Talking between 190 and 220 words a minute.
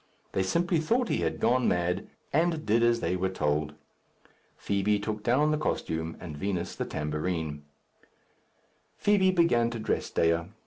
No: average, 150 wpm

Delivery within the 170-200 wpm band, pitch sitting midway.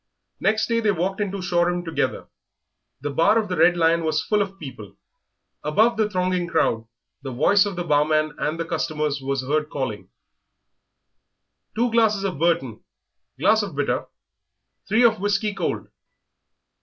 No: average, 155 wpm; medium, 175 Hz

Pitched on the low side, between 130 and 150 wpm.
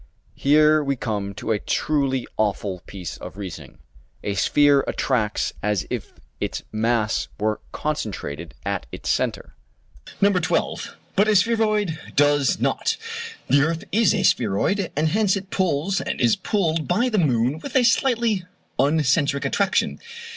No: medium, 145 Hz; average, 145 wpm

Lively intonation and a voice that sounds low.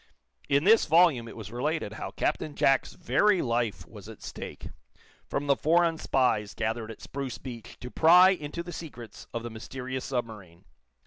Yes: wide, 5.8 semitones; low, 130 Hz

